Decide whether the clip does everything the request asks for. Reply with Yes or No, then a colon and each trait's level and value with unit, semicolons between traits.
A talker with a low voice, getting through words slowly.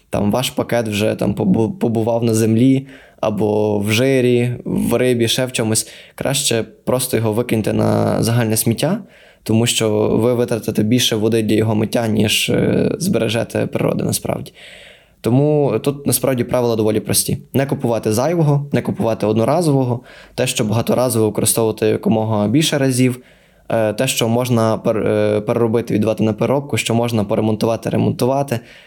No: low, 115 Hz; average, 135 wpm